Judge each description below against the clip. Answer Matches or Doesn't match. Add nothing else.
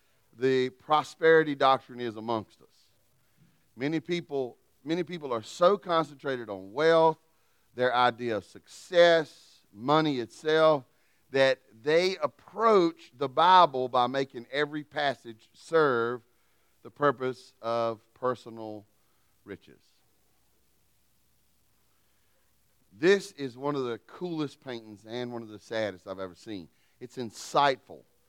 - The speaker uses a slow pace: Matches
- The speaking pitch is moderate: Doesn't match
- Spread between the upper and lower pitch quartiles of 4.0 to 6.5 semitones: Matches